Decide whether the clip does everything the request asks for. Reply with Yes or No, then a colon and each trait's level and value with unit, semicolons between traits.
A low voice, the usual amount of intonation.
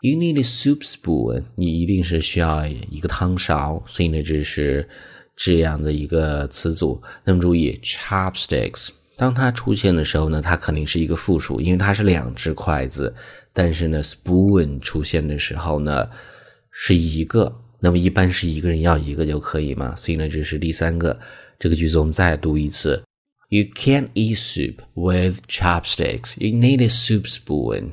Yes: very low, 85 Hz; average, 4.0 semitones